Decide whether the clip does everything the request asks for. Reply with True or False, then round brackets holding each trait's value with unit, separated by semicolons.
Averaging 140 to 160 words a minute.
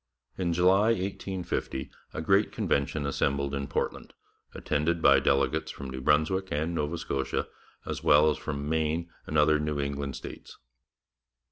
True (145 wpm)